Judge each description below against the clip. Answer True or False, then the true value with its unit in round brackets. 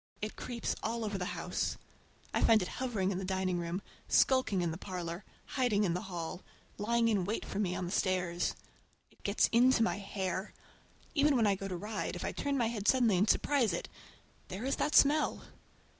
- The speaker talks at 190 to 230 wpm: True (200 wpm)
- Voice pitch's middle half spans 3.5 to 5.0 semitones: True (4.2 semitones)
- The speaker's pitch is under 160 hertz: False (205 Hz)